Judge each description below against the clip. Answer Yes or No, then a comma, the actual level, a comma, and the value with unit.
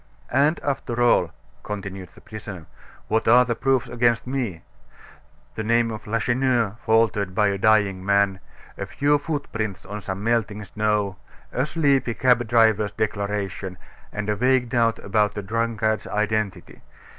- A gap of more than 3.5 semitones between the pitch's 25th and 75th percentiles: No, average, 2.8 semitones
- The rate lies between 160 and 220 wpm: No, average, 145 wpm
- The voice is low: Yes, low, 110 Hz